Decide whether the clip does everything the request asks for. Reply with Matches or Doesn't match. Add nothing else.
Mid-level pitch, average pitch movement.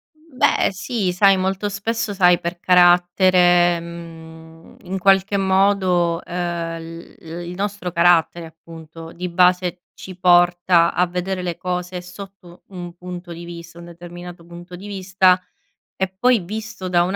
Doesn't match